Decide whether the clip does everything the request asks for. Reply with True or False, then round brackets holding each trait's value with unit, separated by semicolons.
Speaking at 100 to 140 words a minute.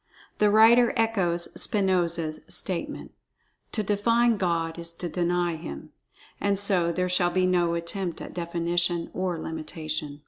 True (135 wpm)